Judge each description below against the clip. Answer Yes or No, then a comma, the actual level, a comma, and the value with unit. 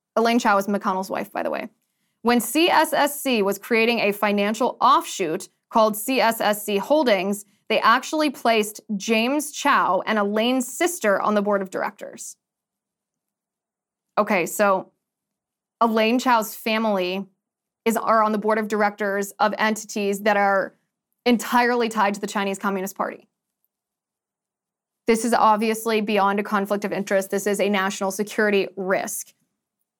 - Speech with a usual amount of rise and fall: No, narrow, 2.3 semitones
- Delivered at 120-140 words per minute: Yes, slow, 135 wpm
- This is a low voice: No, high, 215 Hz